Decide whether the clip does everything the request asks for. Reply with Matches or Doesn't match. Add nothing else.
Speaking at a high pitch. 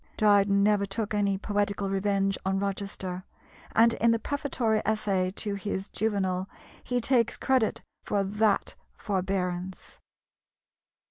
Matches